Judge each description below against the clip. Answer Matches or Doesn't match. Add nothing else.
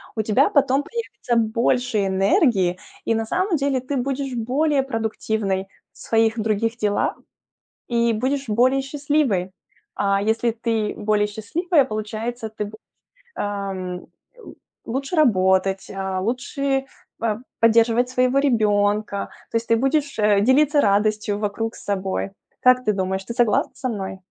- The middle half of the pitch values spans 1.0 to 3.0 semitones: Doesn't match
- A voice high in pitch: Matches